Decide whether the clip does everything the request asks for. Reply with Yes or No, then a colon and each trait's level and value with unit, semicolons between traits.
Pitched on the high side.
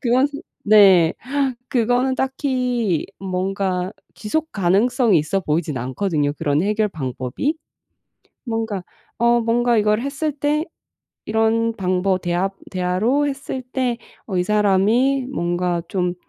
Yes: high, 210 Hz